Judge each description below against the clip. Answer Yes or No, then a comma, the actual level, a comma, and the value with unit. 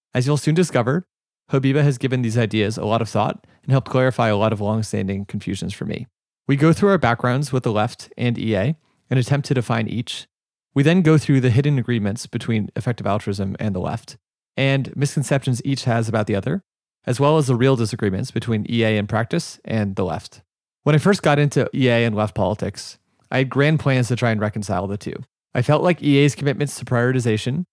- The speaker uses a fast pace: Yes, fast, 210 wpm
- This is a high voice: No, low, 125 Hz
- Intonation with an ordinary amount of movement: Yes, average, 4.4 semitones